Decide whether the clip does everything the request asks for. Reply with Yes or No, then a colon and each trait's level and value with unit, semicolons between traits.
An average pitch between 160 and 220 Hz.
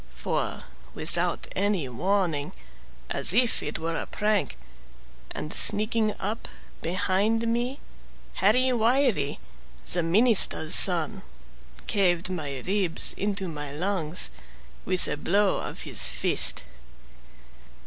Yes: high, 190 Hz